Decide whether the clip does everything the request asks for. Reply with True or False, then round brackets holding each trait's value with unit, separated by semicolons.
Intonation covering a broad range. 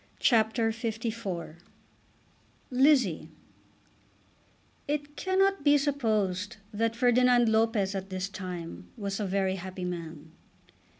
False (4.8 semitones)